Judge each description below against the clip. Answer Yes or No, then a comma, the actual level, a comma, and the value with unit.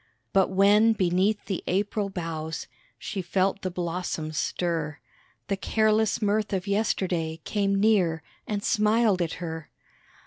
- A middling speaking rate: No, slow, 130 wpm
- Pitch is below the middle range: No, high, 190 Hz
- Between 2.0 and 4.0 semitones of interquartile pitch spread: Yes, average, 3.4 semitones